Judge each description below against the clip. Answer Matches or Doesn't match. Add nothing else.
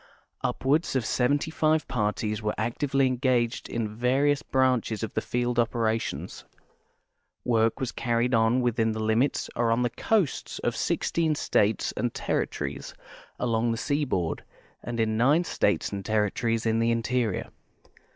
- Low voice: Matches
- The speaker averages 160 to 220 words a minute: Doesn't match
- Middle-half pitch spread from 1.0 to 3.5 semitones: Matches